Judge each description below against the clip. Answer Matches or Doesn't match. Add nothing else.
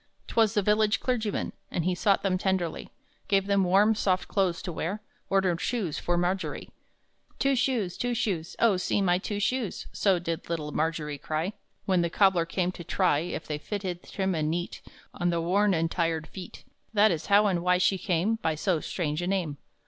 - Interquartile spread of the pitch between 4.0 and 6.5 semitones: Doesn't match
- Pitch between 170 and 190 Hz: Matches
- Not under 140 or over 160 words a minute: Doesn't match